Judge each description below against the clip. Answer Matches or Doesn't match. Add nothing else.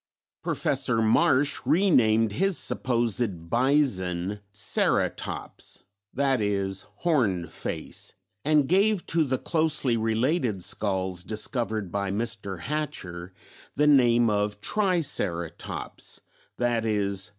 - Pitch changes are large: Matches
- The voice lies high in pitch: Doesn't match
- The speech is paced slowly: Matches